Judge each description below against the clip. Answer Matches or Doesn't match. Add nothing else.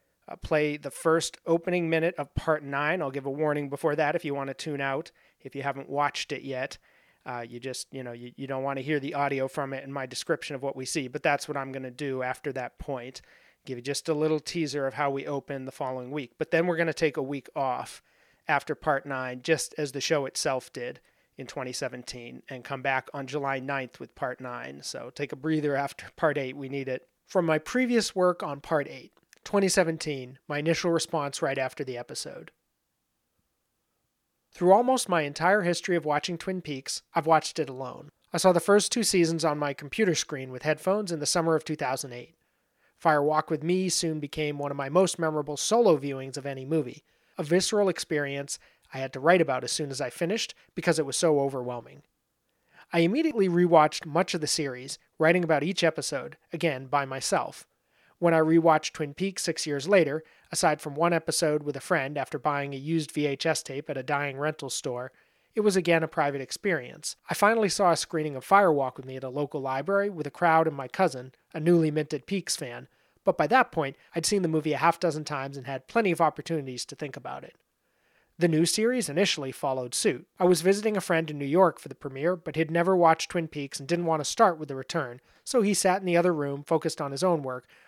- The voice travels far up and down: Doesn't match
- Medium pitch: Matches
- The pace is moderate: Doesn't match